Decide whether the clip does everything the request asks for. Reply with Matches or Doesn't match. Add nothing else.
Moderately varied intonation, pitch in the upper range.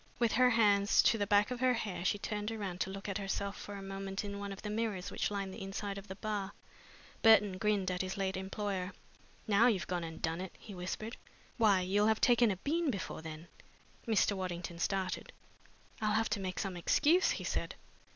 Doesn't match